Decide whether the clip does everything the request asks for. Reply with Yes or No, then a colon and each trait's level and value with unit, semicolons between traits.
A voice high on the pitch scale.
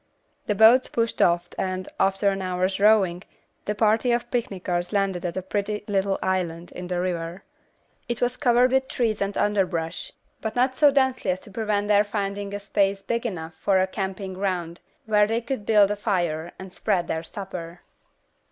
Yes: high, 200 Hz